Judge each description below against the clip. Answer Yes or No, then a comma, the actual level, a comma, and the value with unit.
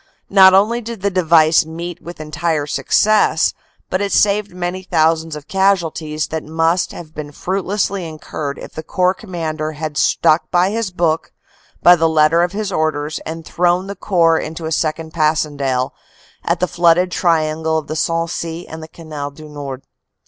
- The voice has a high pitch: No, medium, 165 Hz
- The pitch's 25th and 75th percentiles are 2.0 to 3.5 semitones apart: Yes, average, 2.7 semitones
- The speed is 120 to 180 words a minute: Yes, average, 170 wpm